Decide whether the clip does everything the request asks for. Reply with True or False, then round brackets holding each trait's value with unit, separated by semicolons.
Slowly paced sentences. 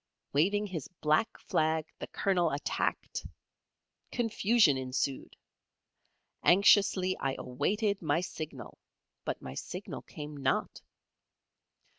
True (95 wpm)